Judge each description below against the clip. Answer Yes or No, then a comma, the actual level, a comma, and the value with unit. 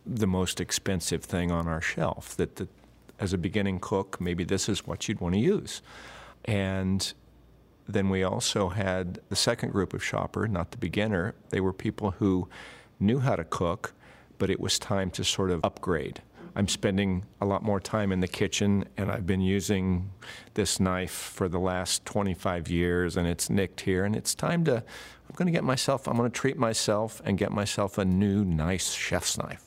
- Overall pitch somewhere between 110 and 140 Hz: No, very low, 95 Hz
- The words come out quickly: No, average, 195 wpm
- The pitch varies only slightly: Yes, narrow, 2.2 semitones